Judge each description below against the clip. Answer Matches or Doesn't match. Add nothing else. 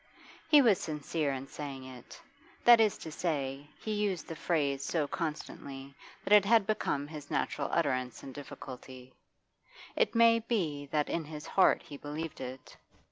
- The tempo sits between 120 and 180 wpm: Matches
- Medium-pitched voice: Matches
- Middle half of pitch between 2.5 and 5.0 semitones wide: Doesn't match